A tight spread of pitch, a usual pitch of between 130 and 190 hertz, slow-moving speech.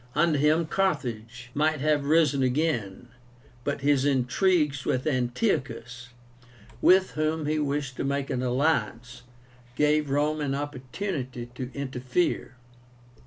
No: average, 3.4 semitones; medium, 140 Hz; slow, 120 wpm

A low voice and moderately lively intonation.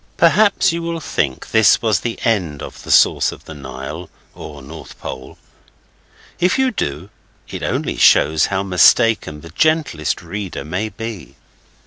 No: very low, 95 Hz; wide, 7.4 semitones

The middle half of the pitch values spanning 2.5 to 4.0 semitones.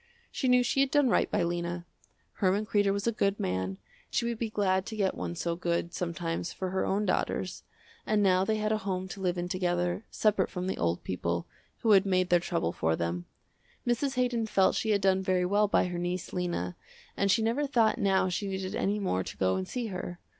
Yes: average, 3.4 semitones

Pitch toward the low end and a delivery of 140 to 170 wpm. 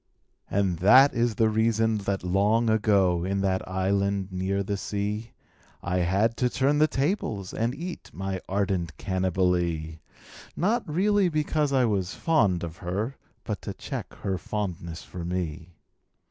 Yes: low, 100 Hz; average, 150 wpm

